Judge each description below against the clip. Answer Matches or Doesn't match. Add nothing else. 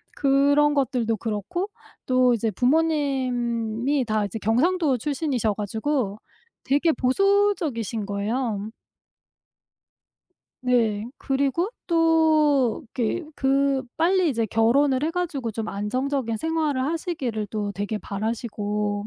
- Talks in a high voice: Matches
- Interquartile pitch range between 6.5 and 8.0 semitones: Doesn't match